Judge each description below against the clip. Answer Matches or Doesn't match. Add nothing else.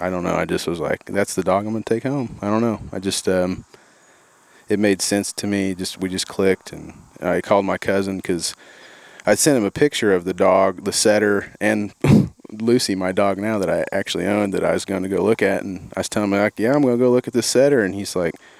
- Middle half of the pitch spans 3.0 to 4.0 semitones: Doesn't match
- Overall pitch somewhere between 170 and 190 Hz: Doesn't match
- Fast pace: Matches